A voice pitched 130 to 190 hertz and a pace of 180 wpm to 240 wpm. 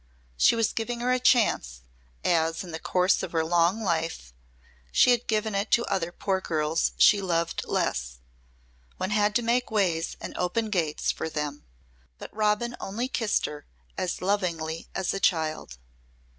No: medium, 185 Hz; average, 165 wpm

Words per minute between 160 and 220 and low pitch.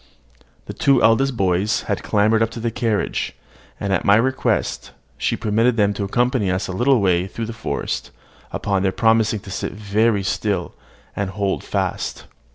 Yes: average, 165 wpm; low, 105 Hz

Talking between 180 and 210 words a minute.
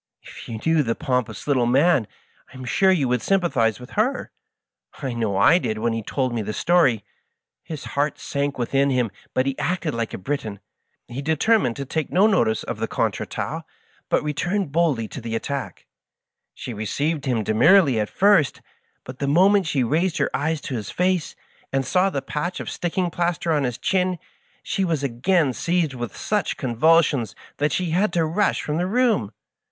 Yes: average, 190 wpm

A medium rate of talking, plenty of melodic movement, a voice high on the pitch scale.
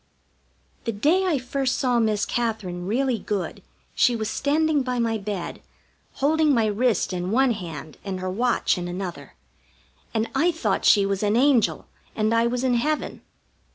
No: average, 165 wpm; average, 4.6 semitones; high, 230 Hz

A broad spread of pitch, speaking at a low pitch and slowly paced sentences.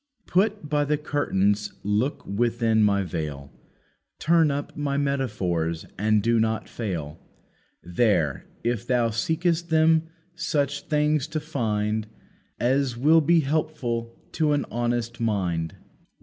Yes: wide, 6.1 semitones; low, 120 Hz; slow, 120 wpm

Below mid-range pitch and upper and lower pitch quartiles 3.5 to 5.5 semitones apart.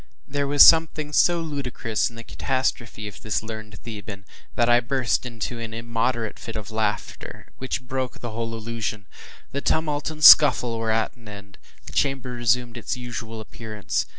No: low, 115 Hz; average, 2.9 semitones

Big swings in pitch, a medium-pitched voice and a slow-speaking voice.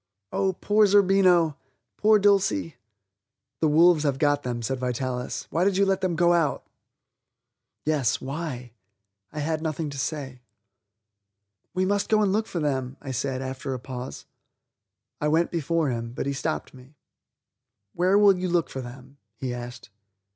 No: wide, 5.7 semitones; medium, 150 Hz; average, 160 wpm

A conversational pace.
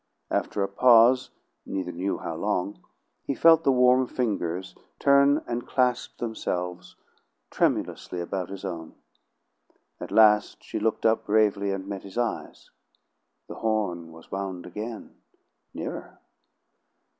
No: slow, 125 wpm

